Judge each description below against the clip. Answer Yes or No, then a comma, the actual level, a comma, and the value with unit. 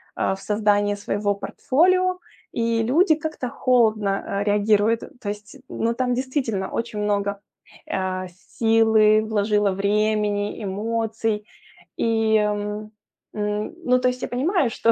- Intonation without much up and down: Yes, narrow, 2.2 semitones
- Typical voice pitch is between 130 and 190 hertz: No, high, 215 Hz